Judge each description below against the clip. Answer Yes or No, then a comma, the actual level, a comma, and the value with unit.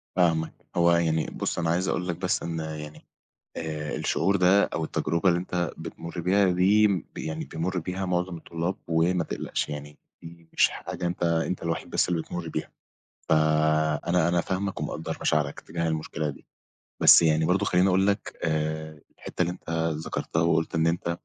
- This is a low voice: Yes, very low, 85 Hz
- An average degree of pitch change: No, narrow, 2.2 semitones